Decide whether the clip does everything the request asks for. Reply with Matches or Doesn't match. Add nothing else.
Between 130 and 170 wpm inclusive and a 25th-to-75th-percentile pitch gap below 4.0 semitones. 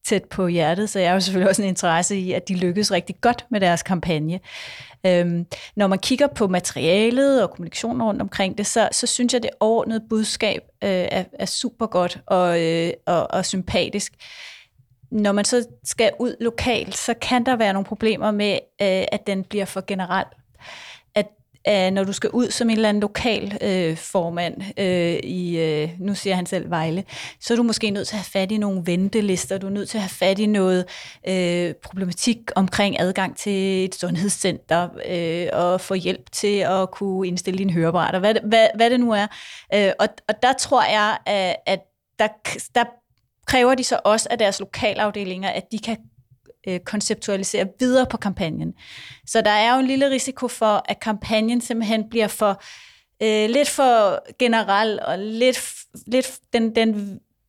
Doesn't match